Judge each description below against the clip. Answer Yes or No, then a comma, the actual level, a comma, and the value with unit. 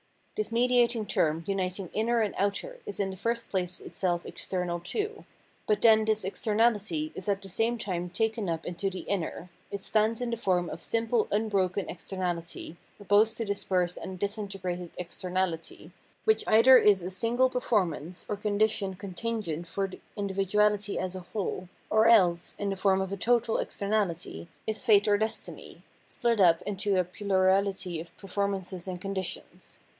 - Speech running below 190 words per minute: Yes, average, 165 wpm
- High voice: Yes, high, 200 Hz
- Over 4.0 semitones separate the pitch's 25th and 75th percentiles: No, average, 3.1 semitones